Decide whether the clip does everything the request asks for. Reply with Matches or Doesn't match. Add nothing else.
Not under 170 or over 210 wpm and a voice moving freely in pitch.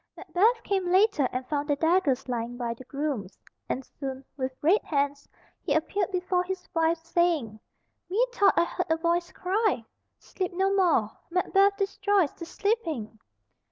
Doesn't match